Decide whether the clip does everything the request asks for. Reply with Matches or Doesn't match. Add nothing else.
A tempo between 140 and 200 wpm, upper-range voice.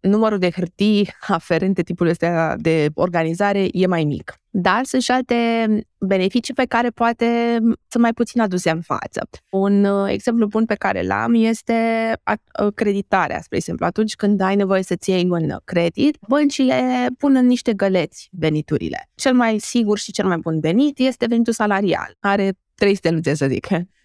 Matches